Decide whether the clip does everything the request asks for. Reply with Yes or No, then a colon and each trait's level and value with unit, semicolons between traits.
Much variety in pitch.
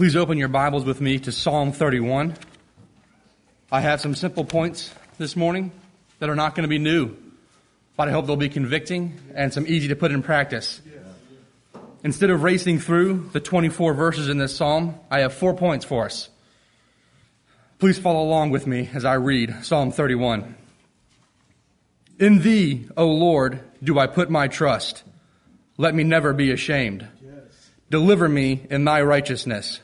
No: average, 3.6 semitones